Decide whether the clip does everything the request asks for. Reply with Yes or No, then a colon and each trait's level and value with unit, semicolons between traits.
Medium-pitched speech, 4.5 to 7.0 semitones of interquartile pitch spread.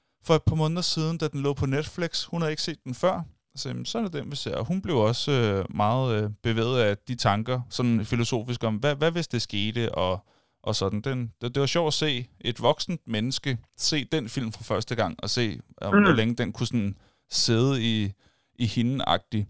No: low, 120 Hz; average, 5.1 semitones